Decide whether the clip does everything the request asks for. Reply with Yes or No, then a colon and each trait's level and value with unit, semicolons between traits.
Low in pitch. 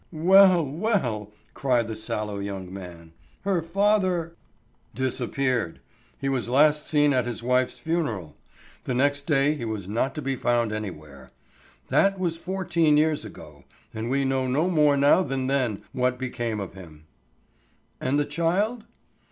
Yes: low, 130 Hz